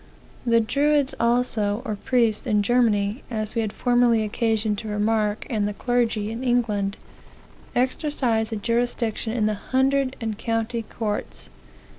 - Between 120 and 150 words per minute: Yes, average, 140 wpm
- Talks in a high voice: Yes, high, 225 Hz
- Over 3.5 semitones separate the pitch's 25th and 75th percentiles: No, narrow, 2.4 semitones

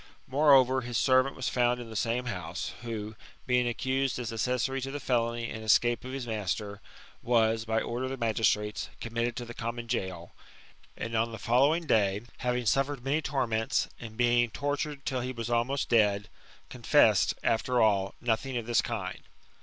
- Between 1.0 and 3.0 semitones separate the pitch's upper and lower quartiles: Yes, narrow, 2.5 semitones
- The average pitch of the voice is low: Yes, low, 120 Hz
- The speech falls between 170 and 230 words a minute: Yes, average, 175 wpm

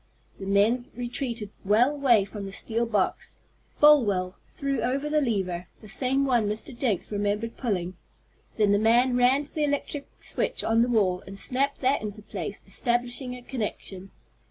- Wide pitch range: No, average, 4.3 semitones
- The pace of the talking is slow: No, average, 165 wpm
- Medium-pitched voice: No, high, 230 Hz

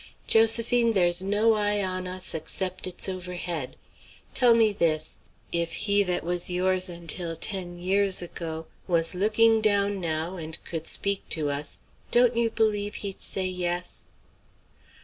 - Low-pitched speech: No, medium, 185 Hz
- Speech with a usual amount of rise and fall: Yes, average, 3.1 semitones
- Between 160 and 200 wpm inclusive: No, average, 145 wpm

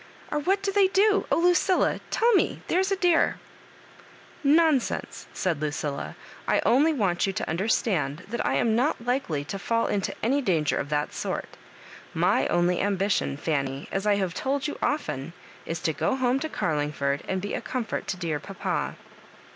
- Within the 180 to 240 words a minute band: Yes, average, 185 wpm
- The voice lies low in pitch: No, high, 205 Hz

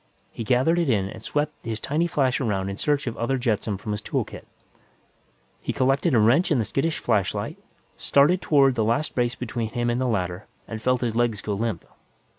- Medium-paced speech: No, fast, 210 wpm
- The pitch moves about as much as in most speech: Yes, average, 3.9 semitones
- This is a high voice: No, low, 120 Hz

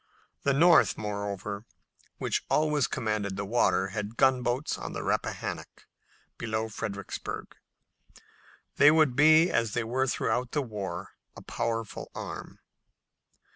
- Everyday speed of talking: No, slow, 125 wpm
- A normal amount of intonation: Yes, average, 4.4 semitones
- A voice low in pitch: Yes, low, 115 Hz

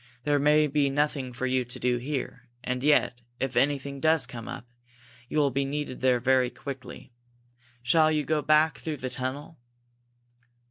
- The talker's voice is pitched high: No, low, 135 Hz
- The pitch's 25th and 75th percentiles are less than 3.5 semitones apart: Yes, average, 2.7 semitones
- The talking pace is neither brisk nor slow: Yes, average, 170 wpm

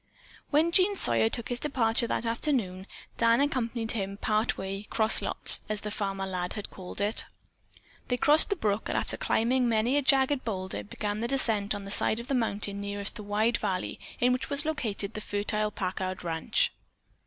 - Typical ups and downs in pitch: Yes, average, 3.8 semitones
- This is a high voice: Yes, high, 215 Hz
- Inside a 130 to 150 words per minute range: No, average, 190 wpm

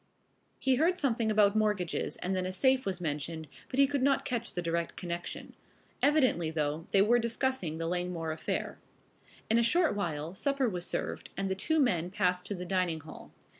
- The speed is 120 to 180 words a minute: No, average, 190 wpm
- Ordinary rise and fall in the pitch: No, wide, 6.3 semitones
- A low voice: No, high, 190 Hz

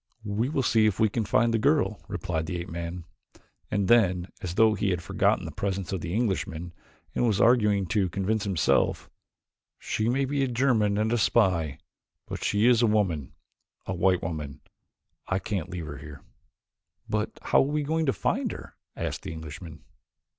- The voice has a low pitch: Yes, low, 100 Hz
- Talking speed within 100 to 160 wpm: No, average, 185 wpm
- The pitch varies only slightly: No, average, 4.7 semitones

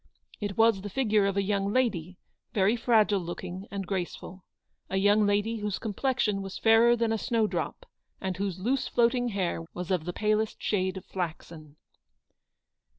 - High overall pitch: Yes, high, 205 Hz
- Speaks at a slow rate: No, average, 170 wpm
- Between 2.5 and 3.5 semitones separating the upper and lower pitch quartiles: Yes, average, 3.0 semitones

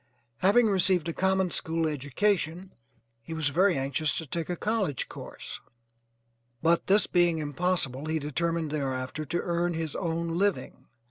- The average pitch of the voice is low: No, medium, 165 Hz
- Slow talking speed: No, average, 145 wpm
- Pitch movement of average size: Yes, average, 3.2 semitones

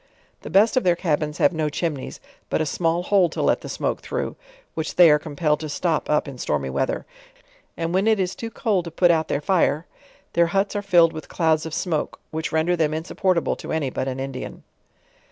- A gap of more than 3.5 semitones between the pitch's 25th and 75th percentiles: No, average, 2.9 semitones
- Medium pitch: Yes, medium, 165 Hz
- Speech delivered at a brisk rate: Yes, fast, 215 wpm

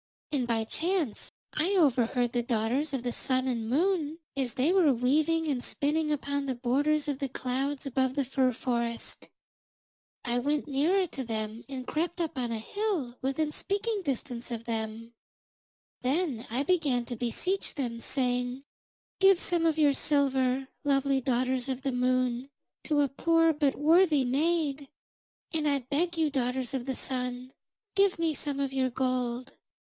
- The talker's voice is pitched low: No, very high, 270 Hz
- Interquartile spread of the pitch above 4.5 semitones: No, average, 3.7 semitones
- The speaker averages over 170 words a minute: No, average, 160 wpm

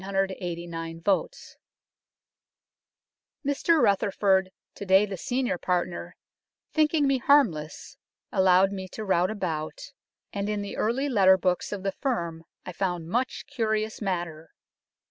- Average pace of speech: No, slow, 120 wpm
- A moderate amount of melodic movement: Yes, average, 3.7 semitones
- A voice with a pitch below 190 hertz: No, high, 195 Hz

